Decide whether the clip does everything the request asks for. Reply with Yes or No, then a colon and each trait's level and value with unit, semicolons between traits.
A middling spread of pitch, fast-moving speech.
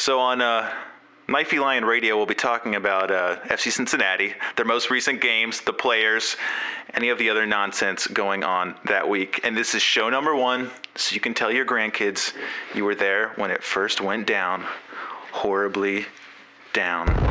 No: average, 3.1 semitones; average, 175 wpm